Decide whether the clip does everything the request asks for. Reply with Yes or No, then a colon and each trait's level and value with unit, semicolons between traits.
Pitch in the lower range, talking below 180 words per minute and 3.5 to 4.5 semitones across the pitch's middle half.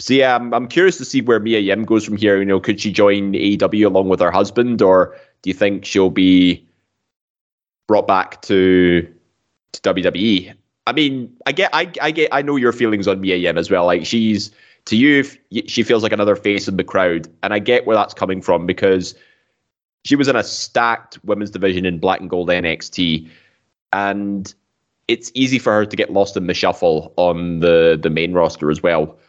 No: low, 100 Hz; fast, 205 wpm; average, 4.2 semitones